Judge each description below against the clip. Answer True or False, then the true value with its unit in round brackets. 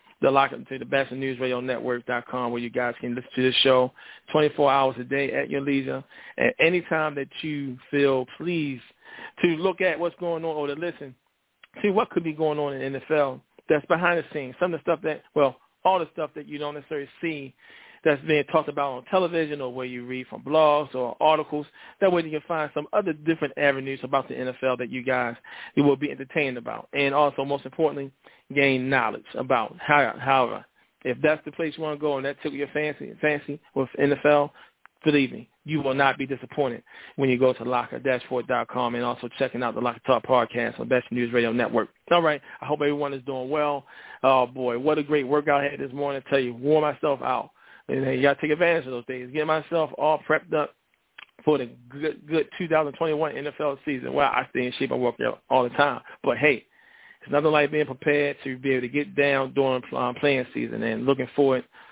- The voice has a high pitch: False (140 Hz)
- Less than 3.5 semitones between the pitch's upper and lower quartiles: True (2.9 semitones)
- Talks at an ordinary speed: False (220 wpm)